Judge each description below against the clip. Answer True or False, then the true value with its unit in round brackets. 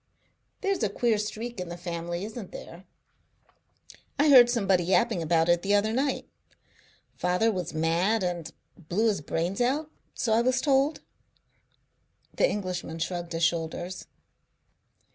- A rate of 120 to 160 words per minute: True (140 wpm)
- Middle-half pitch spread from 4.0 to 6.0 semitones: True (5.2 semitones)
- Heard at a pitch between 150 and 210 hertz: True (190 Hz)